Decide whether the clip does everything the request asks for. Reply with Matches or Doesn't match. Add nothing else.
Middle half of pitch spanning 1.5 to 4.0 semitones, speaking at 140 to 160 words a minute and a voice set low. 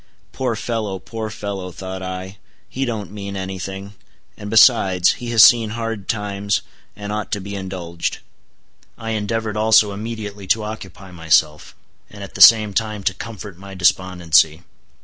Matches